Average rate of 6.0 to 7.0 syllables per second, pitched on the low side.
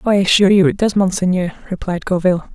No: 6.6 syllables/s; medium, 185 Hz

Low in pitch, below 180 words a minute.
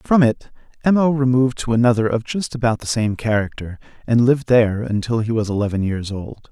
No: low, 115 Hz; fast, 205 wpm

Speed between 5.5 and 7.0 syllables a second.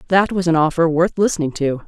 Yes: 6.0 syllables/s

